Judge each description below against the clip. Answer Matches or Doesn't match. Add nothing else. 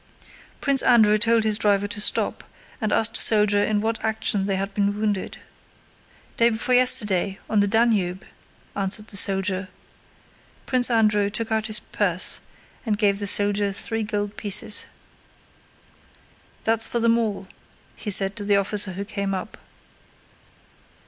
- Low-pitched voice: Doesn't match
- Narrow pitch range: Matches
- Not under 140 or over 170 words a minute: Matches